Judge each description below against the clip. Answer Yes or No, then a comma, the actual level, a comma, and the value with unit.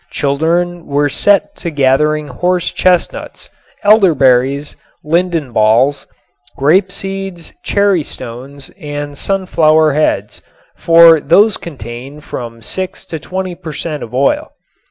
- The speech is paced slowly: Yes, slow, 115 wpm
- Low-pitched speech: No, medium, 155 Hz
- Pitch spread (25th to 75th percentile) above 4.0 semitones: Yes, average, 4.5 semitones